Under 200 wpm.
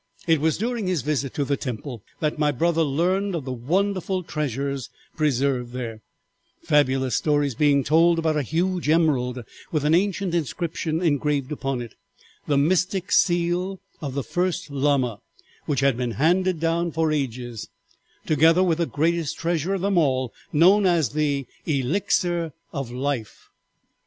Yes: average, 150 wpm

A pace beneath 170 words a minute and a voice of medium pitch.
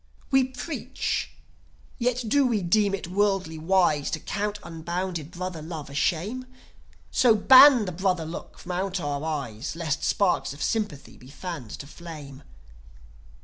Yes: average, 145 wpm; medium, 180 Hz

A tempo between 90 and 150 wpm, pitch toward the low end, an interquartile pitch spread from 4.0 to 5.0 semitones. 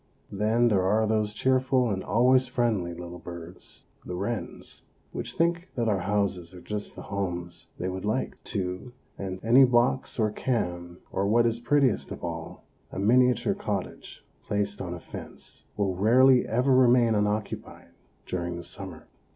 No: average, 160 wpm; low, 105 Hz; average, 4.7 semitones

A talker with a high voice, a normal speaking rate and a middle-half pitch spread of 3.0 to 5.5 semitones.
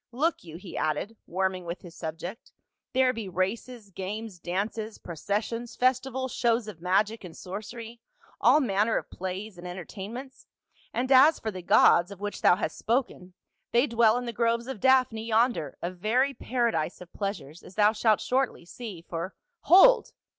Yes: high, 215 Hz; average, 175 wpm; average, 4.7 semitones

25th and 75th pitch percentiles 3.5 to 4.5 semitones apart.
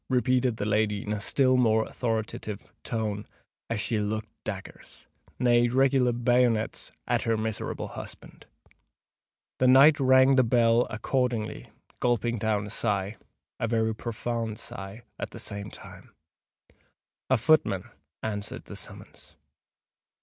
No: average, 2.7 semitones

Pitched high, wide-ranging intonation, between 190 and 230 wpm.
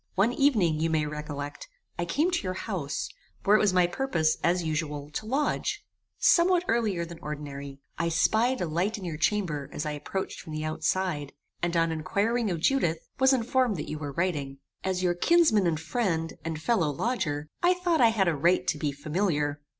No: medium, 170 Hz; wide, 6.2 semitones; average, 195 wpm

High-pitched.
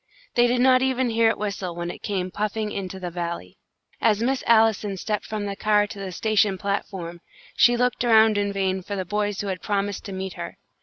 Yes: high, 205 Hz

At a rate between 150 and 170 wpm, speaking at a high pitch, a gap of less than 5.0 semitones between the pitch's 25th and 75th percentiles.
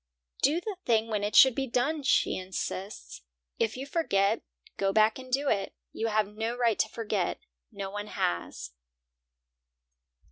Yes: average, 155 wpm; high, 220 Hz; average, 4.2 semitones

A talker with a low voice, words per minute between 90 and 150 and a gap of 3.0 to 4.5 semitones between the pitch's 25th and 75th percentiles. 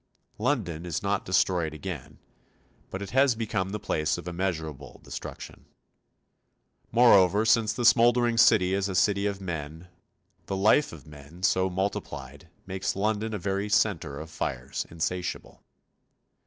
Yes: very low, 95 Hz; average, 140 wpm; average, 3.9 semitones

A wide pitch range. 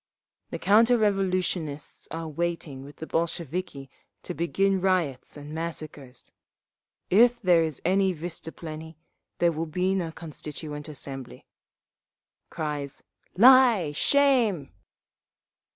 No: average, 4.2 semitones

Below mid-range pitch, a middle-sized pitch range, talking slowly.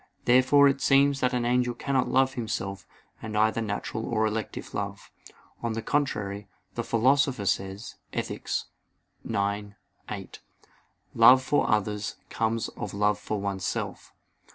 Yes: low, 110 Hz; average, 3.9 semitones; slow, 130 wpm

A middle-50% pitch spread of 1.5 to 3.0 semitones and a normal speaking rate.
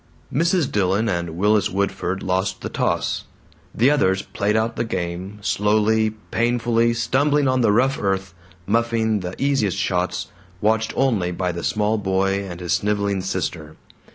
No: average, 3.5 semitones; average, 150 wpm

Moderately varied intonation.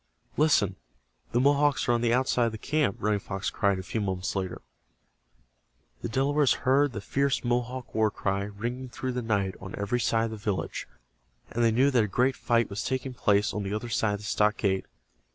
Yes: average, 4.0 semitones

